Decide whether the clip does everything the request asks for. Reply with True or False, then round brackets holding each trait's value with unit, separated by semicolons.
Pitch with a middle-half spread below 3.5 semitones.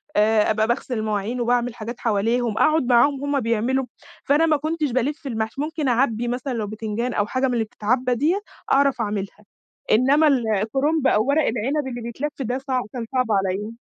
False (3.8 semitones)